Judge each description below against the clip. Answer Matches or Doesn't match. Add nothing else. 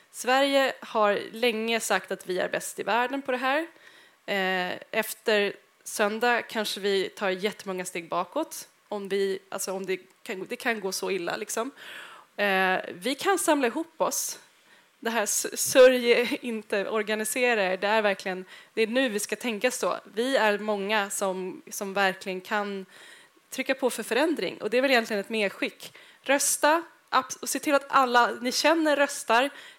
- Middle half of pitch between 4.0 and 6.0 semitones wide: Matches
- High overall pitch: Matches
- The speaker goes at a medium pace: Matches